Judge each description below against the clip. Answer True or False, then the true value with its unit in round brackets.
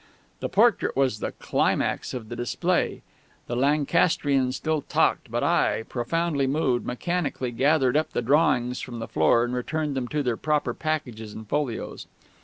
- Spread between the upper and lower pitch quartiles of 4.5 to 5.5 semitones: False (3.9 semitones)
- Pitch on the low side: True (130 Hz)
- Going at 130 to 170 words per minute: True (160 wpm)